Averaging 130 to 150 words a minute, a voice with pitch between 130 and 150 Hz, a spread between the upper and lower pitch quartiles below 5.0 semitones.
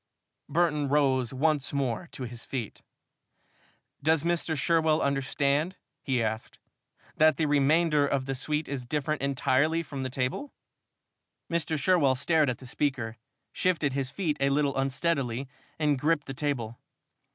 Yes: average, 140 wpm; medium, 140 Hz; average, 3.0 semitones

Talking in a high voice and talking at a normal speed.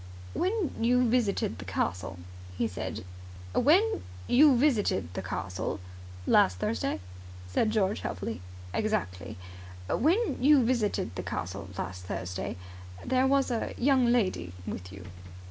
No: high, 210 Hz; slow, 130 wpm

